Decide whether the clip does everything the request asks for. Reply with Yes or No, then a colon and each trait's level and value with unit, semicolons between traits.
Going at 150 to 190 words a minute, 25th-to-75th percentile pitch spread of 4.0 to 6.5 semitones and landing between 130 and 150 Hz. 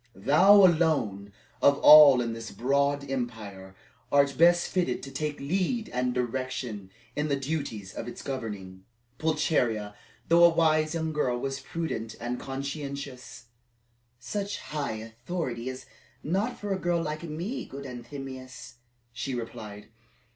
No: slow, 135 wpm; average, 4.6 semitones; low, 135 Hz